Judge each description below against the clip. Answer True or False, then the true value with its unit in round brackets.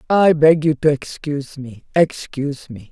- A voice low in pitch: False (145 Hz)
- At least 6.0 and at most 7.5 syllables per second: False (4.6 syllables/s)